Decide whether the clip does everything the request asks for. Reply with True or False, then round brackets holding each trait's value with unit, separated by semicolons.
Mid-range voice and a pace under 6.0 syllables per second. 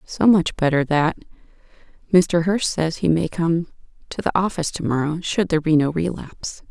True (165 Hz; 5.2 syllables/s)